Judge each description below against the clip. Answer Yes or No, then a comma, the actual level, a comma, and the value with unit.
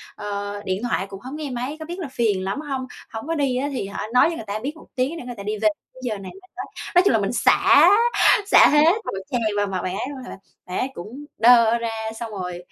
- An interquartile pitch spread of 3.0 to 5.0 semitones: No, wide, 5.5 semitones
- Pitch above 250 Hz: No, high, 235 Hz